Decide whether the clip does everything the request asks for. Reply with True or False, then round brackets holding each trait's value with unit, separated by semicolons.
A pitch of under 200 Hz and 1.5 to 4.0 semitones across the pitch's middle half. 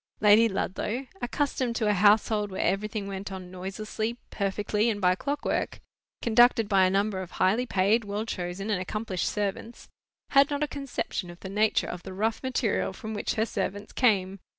False (210 Hz; 2.9 semitones)